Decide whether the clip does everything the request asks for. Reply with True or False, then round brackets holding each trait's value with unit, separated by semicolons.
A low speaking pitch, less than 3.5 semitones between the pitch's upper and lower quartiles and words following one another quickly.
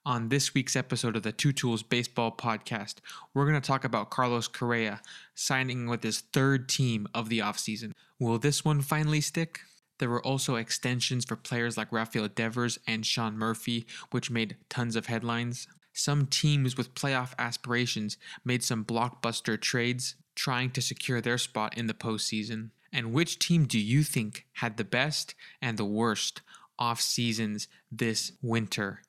False (120 Hz; 2.8 semitones; 165 wpm)